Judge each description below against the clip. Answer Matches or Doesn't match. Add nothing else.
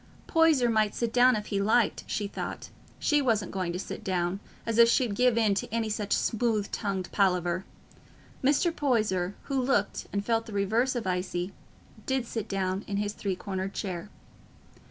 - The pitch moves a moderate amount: Matches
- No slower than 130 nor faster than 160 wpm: Doesn't match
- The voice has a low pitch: Doesn't match